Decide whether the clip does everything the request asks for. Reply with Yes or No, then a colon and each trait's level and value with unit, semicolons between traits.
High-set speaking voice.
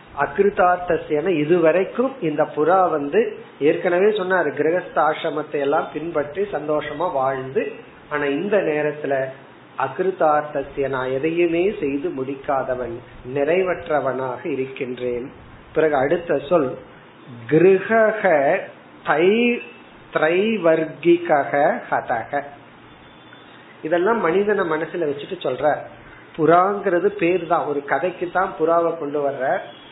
No: medium, 155 Hz